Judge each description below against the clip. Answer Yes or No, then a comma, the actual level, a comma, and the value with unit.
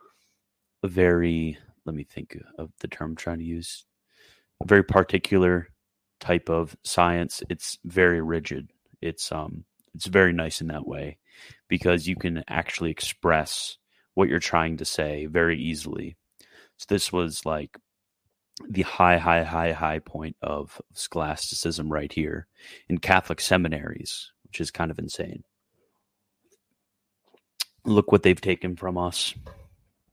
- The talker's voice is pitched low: Yes, very low, 85 Hz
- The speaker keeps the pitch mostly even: Yes, narrow, 2.1 semitones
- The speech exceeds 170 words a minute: No, slow, 135 wpm